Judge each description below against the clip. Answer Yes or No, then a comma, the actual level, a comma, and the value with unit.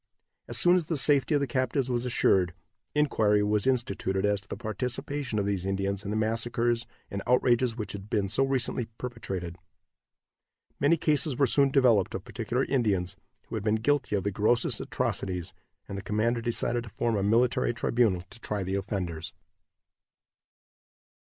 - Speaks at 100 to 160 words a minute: No, average, 170 wpm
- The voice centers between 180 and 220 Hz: No, low, 115 Hz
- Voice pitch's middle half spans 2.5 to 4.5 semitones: Yes, average, 4.1 semitones